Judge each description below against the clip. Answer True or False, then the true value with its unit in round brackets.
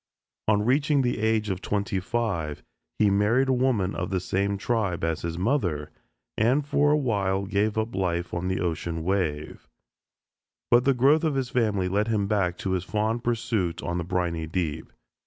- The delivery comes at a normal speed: True (180 wpm)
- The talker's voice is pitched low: True (100 Hz)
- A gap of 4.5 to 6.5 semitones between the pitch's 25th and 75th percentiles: True (4.9 semitones)